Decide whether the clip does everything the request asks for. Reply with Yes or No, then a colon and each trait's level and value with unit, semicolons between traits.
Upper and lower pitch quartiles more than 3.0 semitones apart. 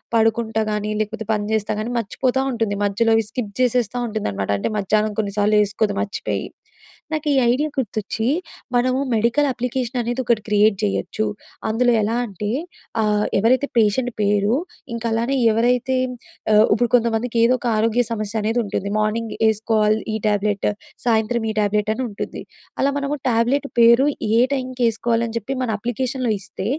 No: narrow, 2.5 semitones